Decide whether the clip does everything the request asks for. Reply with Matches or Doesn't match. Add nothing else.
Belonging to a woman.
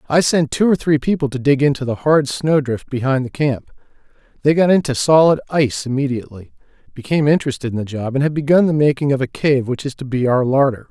Doesn't match